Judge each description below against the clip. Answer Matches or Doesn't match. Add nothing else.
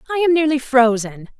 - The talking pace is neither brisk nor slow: Matches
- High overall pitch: Matches